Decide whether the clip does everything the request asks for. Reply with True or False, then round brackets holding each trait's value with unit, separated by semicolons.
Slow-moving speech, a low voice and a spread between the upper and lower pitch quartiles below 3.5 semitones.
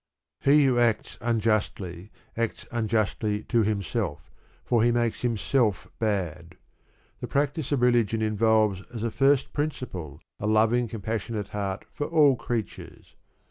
True (130 wpm; 110 Hz; 2.8 semitones)